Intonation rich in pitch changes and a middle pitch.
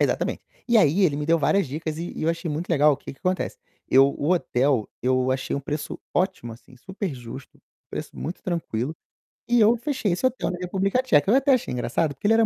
Yes: wide, 6.1 semitones; medium, 165 Hz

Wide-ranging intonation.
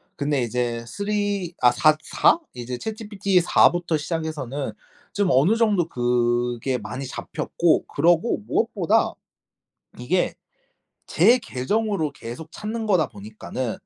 Yes: wide, 8.5 semitones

